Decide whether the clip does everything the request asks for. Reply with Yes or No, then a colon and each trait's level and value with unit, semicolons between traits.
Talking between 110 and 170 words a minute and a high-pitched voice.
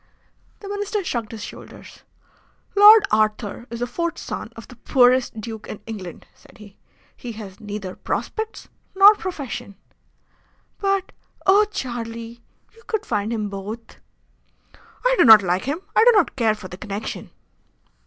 Yes: average, 150 wpm; high, 235 Hz